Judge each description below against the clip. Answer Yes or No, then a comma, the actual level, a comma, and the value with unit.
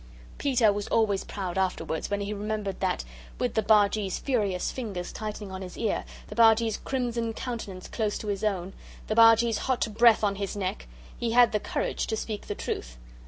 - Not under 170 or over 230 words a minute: Yes, average, 185 wpm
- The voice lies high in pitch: Yes, high, 210 Hz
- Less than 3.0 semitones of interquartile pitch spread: Yes, narrow, 2.6 semitones